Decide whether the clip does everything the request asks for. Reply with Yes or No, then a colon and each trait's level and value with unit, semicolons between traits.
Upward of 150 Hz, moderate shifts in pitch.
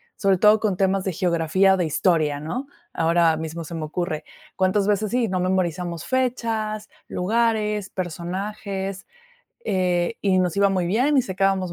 Yes: high, 190 Hz; average, 3.3 semitones